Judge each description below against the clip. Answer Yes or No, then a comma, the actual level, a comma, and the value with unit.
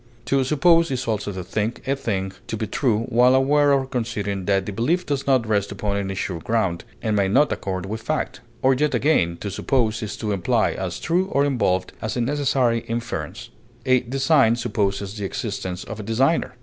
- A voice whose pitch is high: No, low, 115 Hz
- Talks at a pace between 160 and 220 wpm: Yes, average, 200 wpm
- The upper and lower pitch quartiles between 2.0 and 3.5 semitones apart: No, average, 4.9 semitones